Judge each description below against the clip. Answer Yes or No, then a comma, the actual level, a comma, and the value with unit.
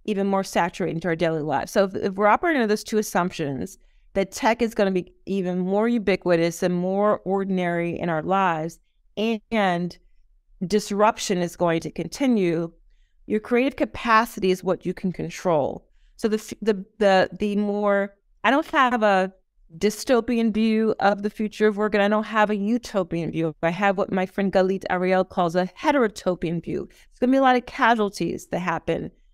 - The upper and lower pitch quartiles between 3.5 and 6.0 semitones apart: No, average, 3.0 semitones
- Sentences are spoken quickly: No, average, 185 wpm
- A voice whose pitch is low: No, high, 195 Hz